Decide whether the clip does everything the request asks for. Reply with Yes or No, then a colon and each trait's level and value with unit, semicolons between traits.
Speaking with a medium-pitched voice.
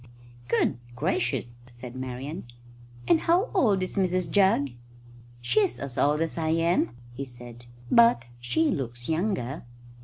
Yes: medium, 145 Hz